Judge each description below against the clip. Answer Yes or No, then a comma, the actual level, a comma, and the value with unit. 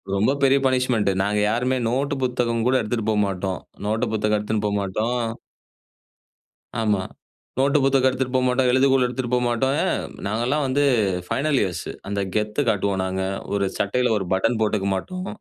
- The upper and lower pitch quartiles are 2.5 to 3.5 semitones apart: No, average, 3.9 semitones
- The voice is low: Yes, low, 120 Hz